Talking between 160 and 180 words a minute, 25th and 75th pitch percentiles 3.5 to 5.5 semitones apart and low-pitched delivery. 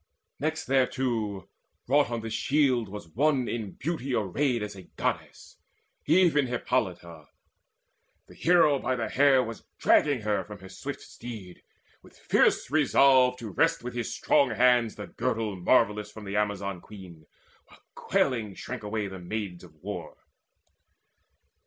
No: average, 145 wpm; average, 4.4 semitones; low, 115 Hz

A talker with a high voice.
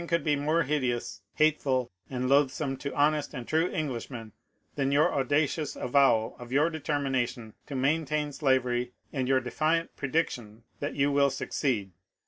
No: medium, 140 Hz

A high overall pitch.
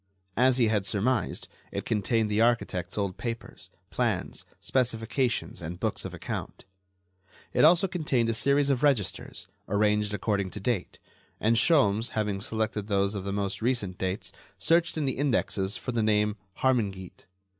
No: low, 110 Hz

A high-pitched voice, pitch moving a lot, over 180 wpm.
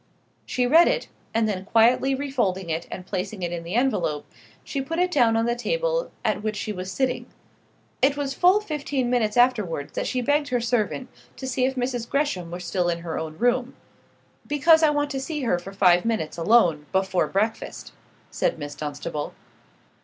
Yes: high, 230 Hz; wide, 6.9 semitones; average, 190 wpm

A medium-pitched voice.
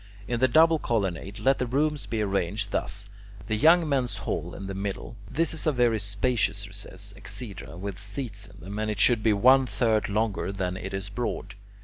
No: low, 105 Hz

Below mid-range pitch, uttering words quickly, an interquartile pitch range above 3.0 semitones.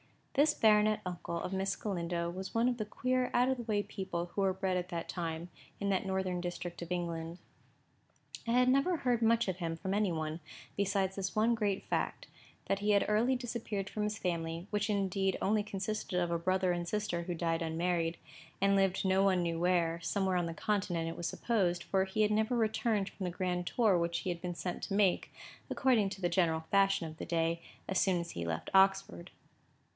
No: high, 190 Hz; fast, 210 wpm; average, 3.5 semitones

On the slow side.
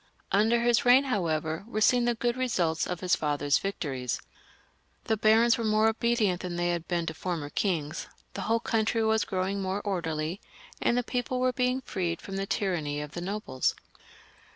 No: average, 180 wpm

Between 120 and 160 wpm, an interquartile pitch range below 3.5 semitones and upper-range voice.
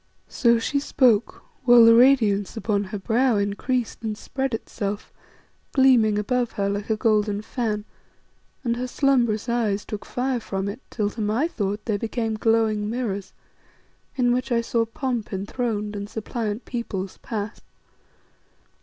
Yes: average, 145 wpm; average, 2.9 semitones; high, 225 Hz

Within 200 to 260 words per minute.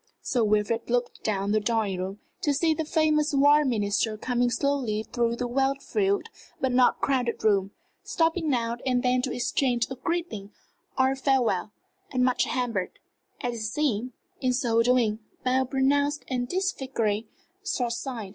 No: average, 165 wpm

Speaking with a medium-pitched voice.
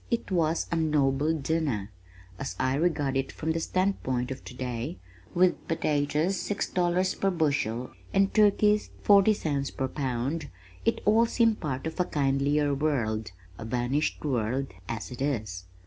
Yes: medium, 145 Hz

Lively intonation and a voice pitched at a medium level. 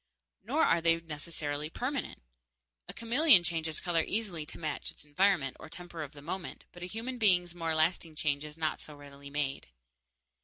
No: average, 3.2 semitones; medium, 165 Hz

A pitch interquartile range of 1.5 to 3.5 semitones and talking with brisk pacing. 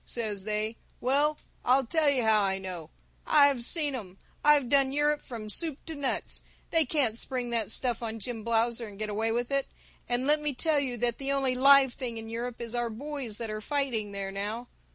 No: average, 4.0 semitones; fast, 210 wpm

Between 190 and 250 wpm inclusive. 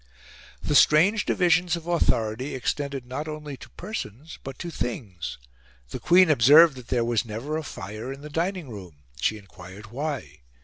No: average, 165 wpm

